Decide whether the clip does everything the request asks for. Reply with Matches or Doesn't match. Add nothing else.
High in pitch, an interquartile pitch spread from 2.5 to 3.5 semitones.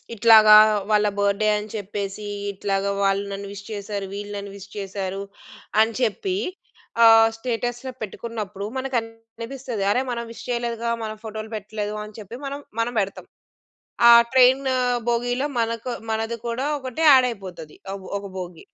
Matches